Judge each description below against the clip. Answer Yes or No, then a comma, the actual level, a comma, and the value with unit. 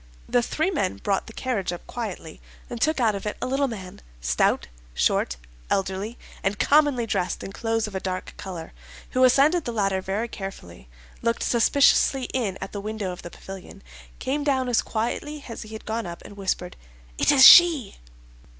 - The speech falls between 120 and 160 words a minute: No, average, 185 wpm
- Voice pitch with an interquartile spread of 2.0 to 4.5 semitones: No, average, 5.1 semitones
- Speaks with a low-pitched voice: No, high, 220 Hz